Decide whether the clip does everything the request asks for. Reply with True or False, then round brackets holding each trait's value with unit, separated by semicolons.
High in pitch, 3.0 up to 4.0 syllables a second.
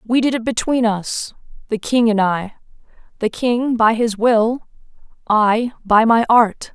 True (225 Hz; 3.9 syllables/s)